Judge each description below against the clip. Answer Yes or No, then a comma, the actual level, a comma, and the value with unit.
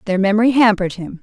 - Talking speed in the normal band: Yes, average, 195 wpm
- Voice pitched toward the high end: Yes, high, 210 Hz